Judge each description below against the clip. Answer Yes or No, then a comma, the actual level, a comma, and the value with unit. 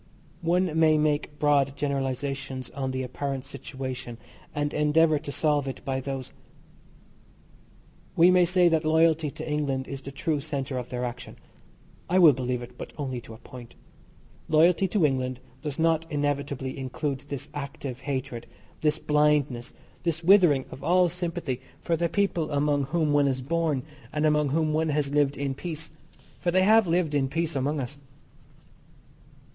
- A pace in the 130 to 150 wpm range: No, average, 160 wpm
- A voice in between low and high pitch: Yes, medium, 145 Hz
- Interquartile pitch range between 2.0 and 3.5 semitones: Yes, average, 3.2 semitones